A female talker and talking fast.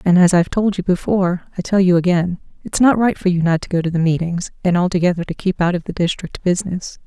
Yes: female; fast, 255 wpm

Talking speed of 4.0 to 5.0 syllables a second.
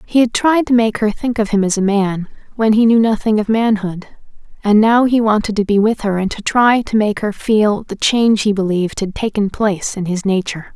No: 5.3 syllables/s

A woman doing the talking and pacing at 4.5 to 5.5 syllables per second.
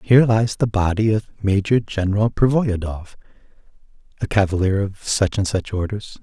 No: male; 5.3 syllables/s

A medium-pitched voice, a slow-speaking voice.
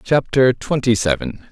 No: low, 125 Hz; slow, 120 wpm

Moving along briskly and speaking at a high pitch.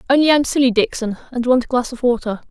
Yes: fast, 240 wpm; very high, 250 Hz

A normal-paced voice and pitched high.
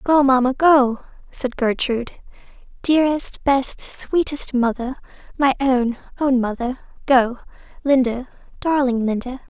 No: slow, 100 wpm; very high, 260 Hz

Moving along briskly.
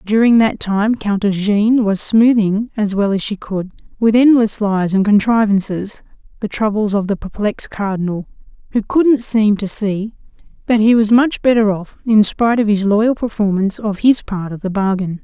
No: average, 180 wpm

